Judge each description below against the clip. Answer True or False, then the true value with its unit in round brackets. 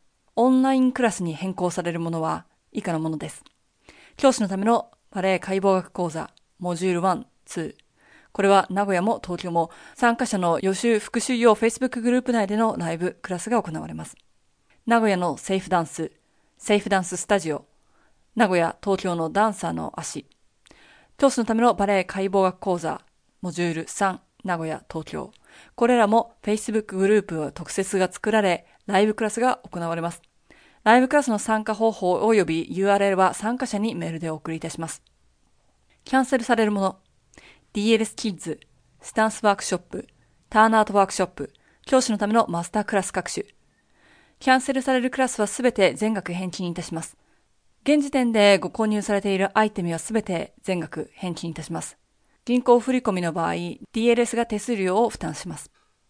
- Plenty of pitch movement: False (4.4 semitones)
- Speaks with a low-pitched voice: False (200 Hz)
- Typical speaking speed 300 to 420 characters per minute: True (365 characters per minute)